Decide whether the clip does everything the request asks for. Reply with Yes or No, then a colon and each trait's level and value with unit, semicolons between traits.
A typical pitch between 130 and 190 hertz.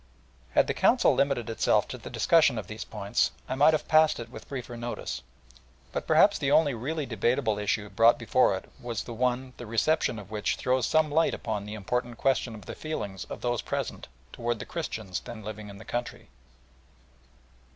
No: low, 120 Hz